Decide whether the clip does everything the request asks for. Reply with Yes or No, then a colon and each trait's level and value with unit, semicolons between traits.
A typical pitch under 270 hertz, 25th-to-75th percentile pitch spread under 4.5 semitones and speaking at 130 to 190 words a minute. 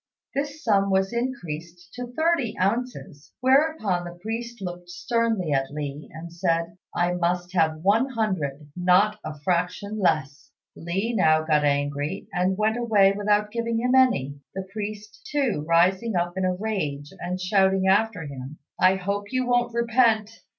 No: high, 190 Hz; average, 5.0 semitones; average, 155 wpm